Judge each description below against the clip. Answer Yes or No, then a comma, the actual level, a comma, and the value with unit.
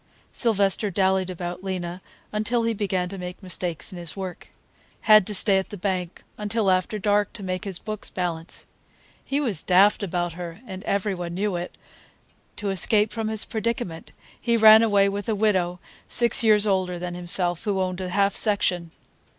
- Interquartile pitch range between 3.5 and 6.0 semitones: No, average, 2.9 semitones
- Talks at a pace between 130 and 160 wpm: No, average, 180 wpm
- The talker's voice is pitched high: Yes, high, 195 Hz